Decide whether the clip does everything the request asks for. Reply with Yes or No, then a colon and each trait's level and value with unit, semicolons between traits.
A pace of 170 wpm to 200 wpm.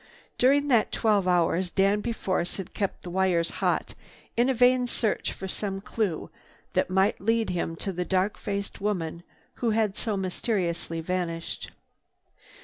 No: average, 150 wpm